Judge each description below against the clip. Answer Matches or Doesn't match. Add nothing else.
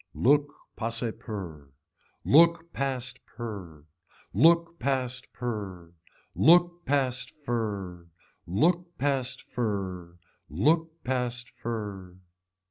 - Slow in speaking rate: Matches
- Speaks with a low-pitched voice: Matches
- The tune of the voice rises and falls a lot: Matches